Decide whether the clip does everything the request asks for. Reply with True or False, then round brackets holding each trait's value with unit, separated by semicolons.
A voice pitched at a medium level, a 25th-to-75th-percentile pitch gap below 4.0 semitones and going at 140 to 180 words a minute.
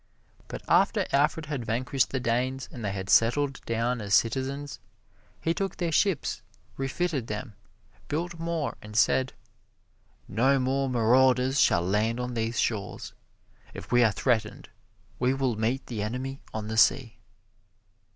False (125 Hz; 3.4 semitones; 145 wpm)